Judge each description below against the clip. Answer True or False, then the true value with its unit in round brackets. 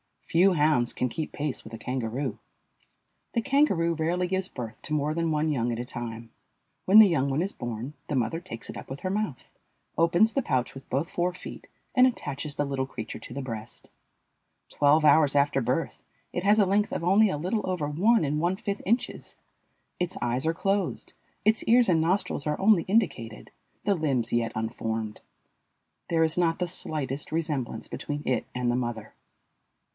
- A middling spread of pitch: False (6.4 semitones)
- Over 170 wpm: True (190 wpm)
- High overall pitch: False (155 Hz)